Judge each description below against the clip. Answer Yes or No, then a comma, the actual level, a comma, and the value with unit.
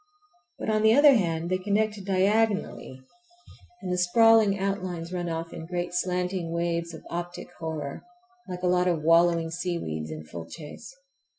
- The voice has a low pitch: No, medium, 180 Hz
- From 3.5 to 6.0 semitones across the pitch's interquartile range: No, average, 2.8 semitones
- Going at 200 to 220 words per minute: No, average, 160 wpm